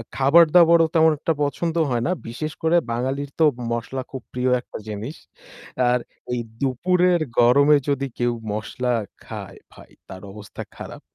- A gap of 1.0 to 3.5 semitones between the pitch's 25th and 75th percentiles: No, average, 4.9 semitones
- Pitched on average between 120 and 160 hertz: Yes, low, 135 Hz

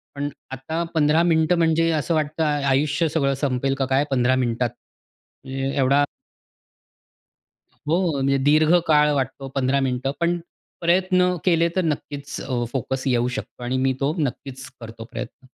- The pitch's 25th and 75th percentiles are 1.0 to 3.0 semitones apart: No, average, 3.4 semitones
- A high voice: No, medium, 140 Hz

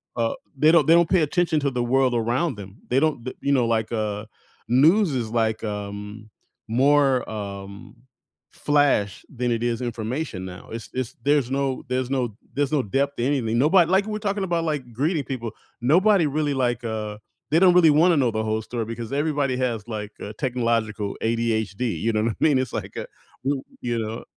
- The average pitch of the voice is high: No, low, 125 Hz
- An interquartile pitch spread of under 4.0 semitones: No, average, 4.7 semitones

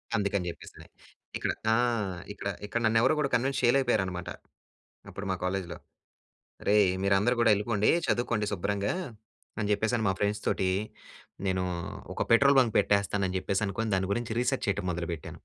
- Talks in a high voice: No, low, 100 Hz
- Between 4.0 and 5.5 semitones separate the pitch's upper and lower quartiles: No, average, 3.4 semitones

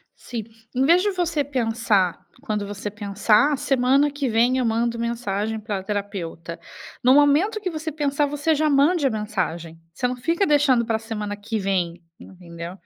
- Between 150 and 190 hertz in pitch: No, high, 235 Hz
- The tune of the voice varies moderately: No, wide, 5.9 semitones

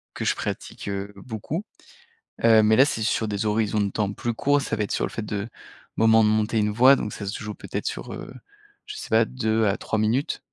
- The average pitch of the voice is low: Yes, low, 110 Hz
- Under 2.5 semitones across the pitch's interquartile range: Yes, narrow, 1.4 semitones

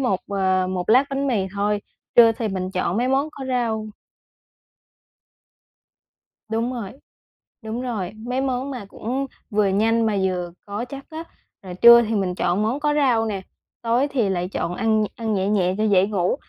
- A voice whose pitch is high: Yes, high, 220 Hz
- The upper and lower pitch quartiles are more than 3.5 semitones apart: Yes, average, 4.3 semitones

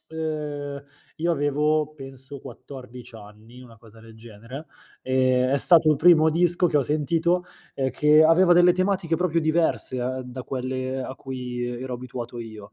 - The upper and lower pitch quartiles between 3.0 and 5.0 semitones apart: Yes, average, 4.0 semitones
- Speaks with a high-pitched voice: No, low, 135 Hz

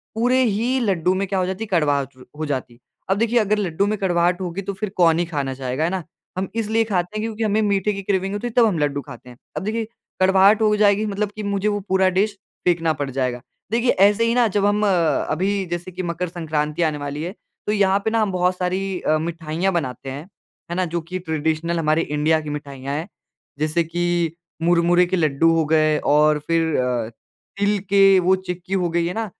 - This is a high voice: No, medium, 180 Hz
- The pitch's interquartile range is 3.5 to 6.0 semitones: Yes, average, 4.4 semitones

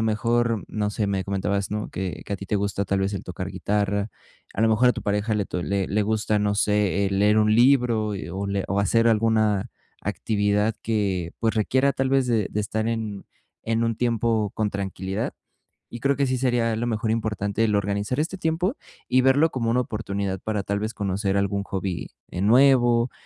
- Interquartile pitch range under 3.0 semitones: Yes, narrow, 2.6 semitones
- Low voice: Yes, low, 105 Hz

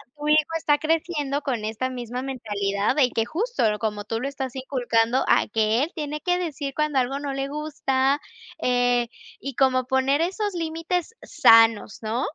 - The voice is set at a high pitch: Yes, very high, 270 Hz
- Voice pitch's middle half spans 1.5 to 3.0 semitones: No, average, 4.0 semitones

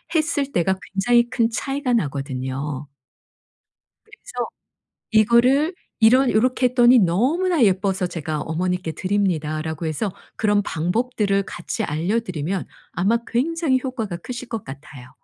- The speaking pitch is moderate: No, high, 205 Hz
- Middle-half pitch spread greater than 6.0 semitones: Yes, wide, 7.1 semitones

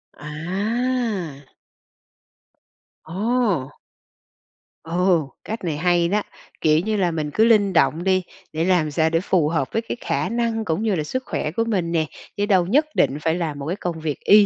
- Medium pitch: Yes, medium, 180 Hz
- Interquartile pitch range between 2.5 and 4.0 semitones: No, average, 5.1 semitones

